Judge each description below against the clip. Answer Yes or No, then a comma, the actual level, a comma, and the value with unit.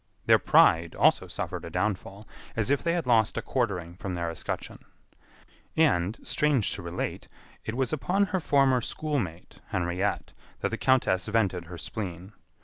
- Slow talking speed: No, average, 155 wpm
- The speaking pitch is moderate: No, low, 105 Hz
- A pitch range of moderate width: No, wide, 6.9 semitones